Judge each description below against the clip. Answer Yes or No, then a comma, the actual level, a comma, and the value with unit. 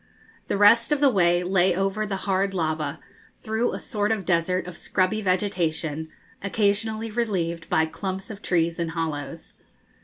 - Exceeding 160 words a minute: No, average, 155 wpm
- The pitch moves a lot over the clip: No, average, 3.9 semitones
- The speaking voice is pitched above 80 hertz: Yes, medium, 185 Hz